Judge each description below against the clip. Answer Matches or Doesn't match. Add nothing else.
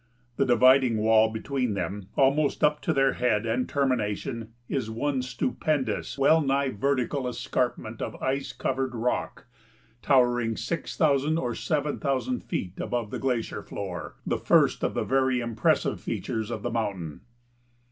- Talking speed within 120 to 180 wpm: Matches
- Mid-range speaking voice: Doesn't match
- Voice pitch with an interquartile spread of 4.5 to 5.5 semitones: Doesn't match